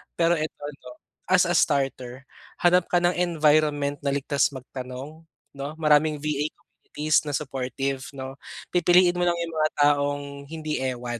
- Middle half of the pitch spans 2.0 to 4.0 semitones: Yes, average, 2.9 semitones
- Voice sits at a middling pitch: Yes, medium, 150 Hz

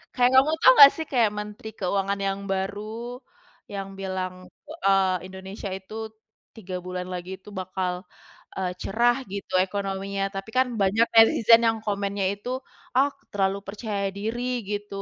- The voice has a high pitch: Yes, high, 200 Hz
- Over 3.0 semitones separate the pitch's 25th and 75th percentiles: No, narrow, 2.5 semitones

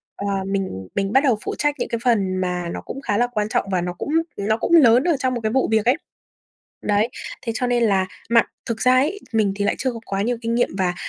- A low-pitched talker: No, high, 225 Hz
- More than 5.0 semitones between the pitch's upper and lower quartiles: No, average, 3.9 semitones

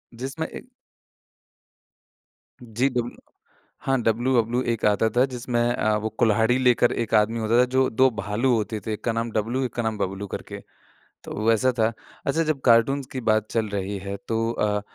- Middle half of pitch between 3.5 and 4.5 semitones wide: No, average, 2.7 semitones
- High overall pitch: No, low, 115 Hz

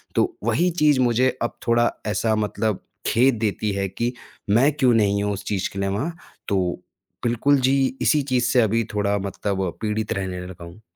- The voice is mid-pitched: No, low, 110 Hz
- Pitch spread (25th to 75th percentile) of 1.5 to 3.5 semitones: No, average, 4.0 semitones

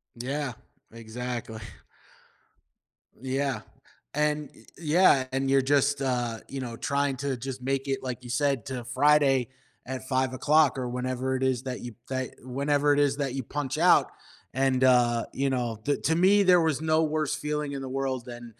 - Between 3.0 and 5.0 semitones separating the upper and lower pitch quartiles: No, narrow, 2.4 semitones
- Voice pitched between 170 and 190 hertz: No, low, 135 Hz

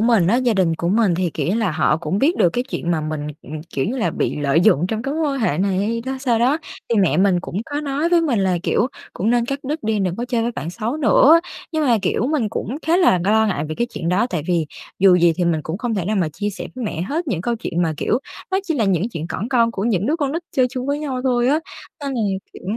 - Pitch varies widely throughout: Yes, wide, 6.5 semitones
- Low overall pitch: No, high, 220 Hz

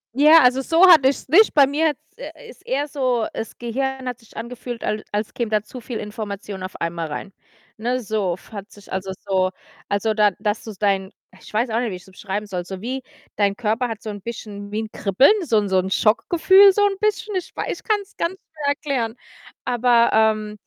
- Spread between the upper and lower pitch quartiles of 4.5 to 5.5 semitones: Yes, average, 4.8 semitones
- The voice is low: No, high, 225 Hz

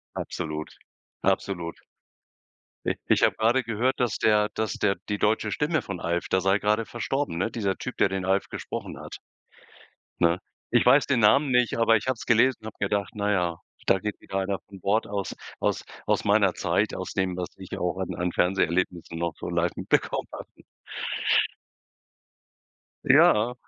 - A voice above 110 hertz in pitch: No, low, 100 Hz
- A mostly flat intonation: No, average, 3.7 semitones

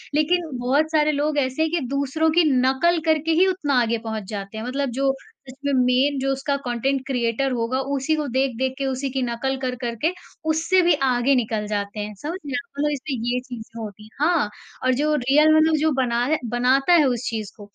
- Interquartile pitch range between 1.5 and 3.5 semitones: No, average, 3.9 semitones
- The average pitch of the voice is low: No, very high, 270 Hz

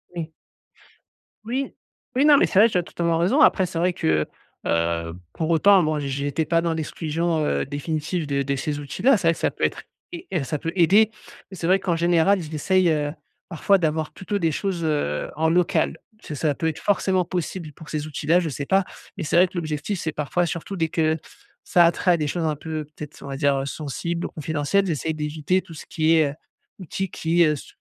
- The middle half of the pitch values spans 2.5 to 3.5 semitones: Yes, average, 3.1 semitones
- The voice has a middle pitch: Yes, medium, 160 Hz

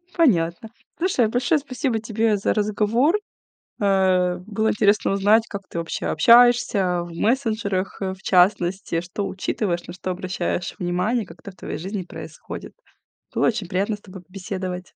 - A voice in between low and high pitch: No, high, 200 Hz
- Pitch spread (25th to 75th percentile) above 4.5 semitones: No, average, 3.5 semitones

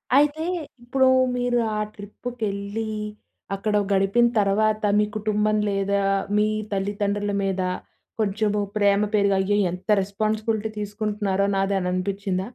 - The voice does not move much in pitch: Yes, narrow, 1.5 semitones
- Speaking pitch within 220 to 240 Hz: No, high, 205 Hz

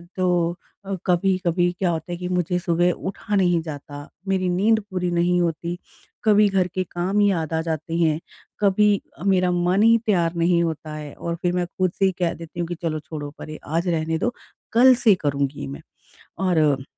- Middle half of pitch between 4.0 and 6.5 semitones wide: No, narrow, 2.4 semitones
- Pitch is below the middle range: No, medium, 175 Hz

